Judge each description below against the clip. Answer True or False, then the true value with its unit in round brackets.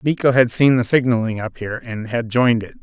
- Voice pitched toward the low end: True (120 Hz)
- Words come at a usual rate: False (235 wpm)